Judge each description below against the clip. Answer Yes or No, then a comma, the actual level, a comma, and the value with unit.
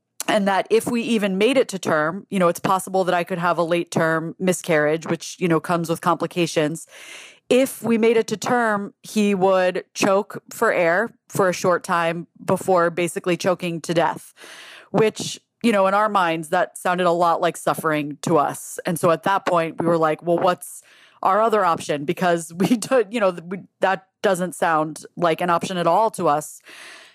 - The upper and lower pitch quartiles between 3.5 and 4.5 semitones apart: No, average, 3.0 semitones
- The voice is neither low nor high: Yes, medium, 180 Hz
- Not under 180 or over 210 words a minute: Yes, average, 195 wpm